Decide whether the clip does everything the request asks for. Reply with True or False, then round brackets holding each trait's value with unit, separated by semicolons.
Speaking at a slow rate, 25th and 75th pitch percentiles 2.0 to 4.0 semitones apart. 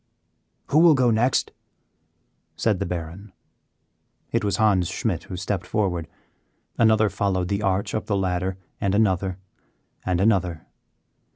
True (130 wpm; 3.0 semitones)